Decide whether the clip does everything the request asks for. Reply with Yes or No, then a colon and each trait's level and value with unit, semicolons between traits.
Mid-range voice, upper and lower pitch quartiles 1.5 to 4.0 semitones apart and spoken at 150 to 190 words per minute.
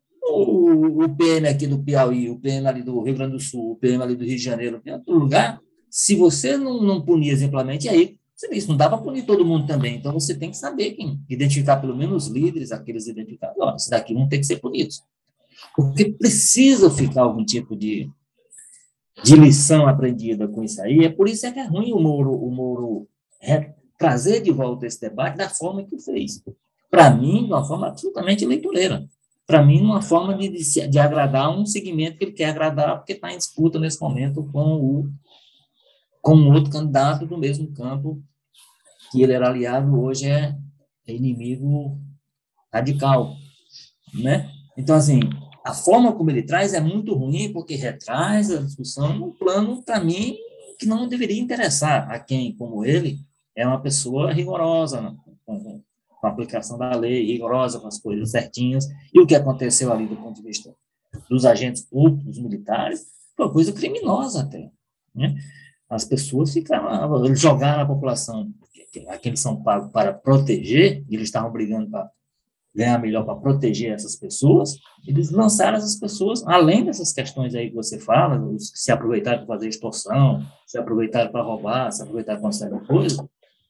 No: medium, 145 Hz; average, 5.2 semitones; average, 180 wpm